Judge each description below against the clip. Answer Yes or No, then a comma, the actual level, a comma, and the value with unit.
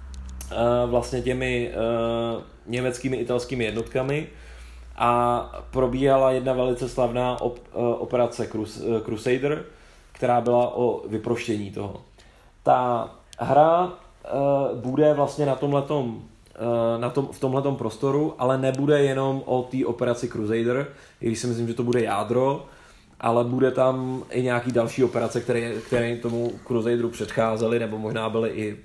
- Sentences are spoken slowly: No, average, 130 wpm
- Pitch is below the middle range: Yes, low, 120 Hz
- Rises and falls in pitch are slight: Yes, narrow, 2.3 semitones